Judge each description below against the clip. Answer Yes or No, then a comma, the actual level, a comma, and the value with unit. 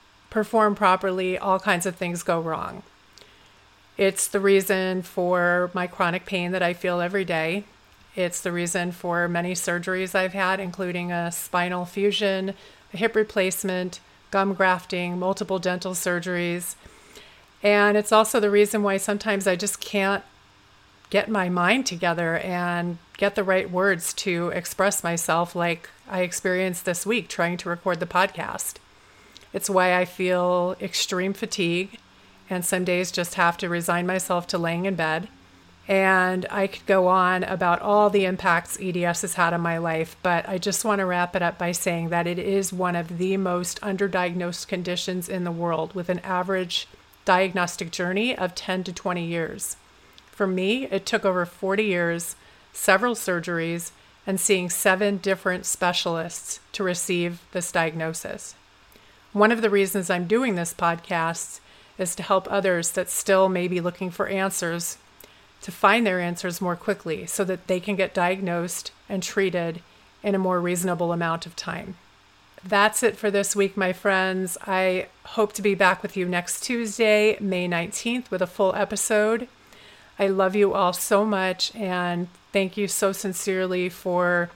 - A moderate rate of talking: Yes, average, 160 wpm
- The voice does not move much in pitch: Yes, narrow, 2.0 semitones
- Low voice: No, medium, 185 Hz